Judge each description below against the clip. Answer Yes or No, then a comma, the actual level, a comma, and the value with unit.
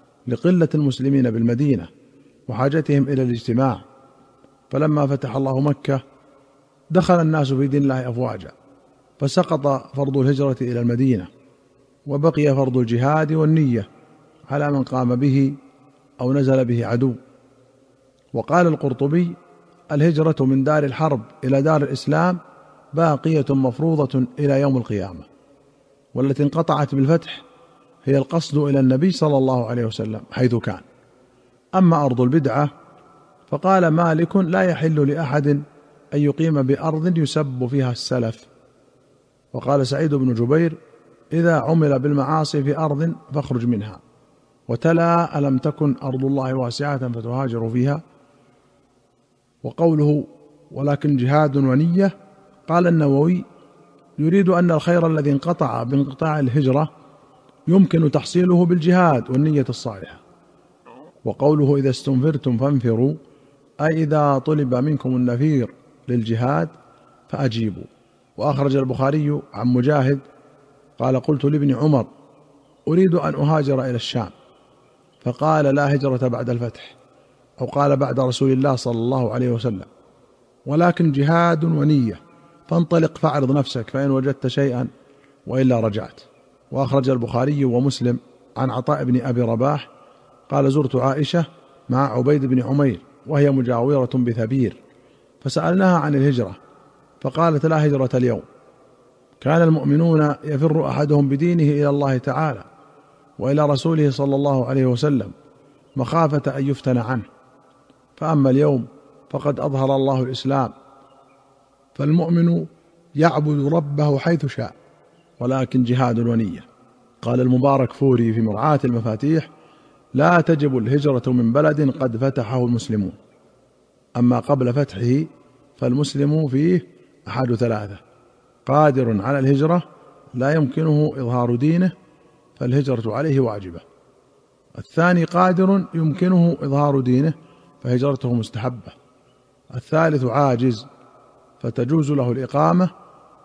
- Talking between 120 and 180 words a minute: No, average, 110 wpm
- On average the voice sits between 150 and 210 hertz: No, medium, 140 Hz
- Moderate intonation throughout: Yes, average, 3.0 semitones